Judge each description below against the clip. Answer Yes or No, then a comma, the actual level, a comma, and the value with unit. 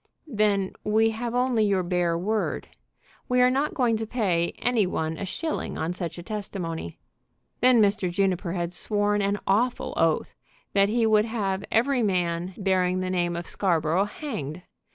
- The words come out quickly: No, average, 165 wpm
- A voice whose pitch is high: Yes, high, 200 Hz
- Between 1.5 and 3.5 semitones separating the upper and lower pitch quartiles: No, average, 4.0 semitones